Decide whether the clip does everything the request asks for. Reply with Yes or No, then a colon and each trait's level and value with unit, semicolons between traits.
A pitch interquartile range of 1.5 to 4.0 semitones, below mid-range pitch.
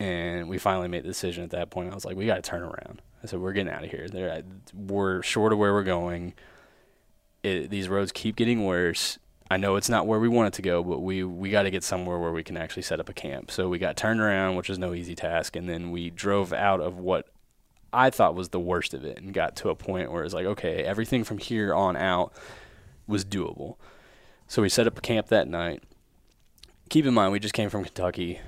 Yes: narrow, 2.5 semitones; very low, 95 Hz